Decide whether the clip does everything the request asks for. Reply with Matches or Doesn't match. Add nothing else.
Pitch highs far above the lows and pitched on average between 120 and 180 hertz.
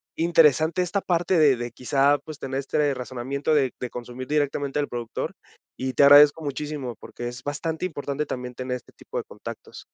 Doesn't match